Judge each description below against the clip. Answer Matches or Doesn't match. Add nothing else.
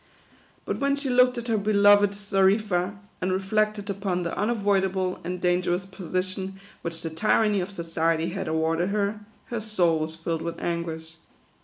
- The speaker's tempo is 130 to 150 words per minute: Doesn't match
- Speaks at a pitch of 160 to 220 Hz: Matches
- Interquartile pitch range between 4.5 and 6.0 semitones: Doesn't match